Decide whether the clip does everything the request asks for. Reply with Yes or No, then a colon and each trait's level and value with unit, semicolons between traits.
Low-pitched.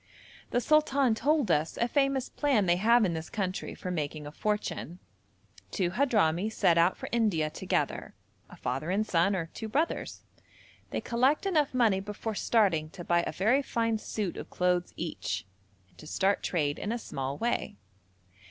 No: high, 205 Hz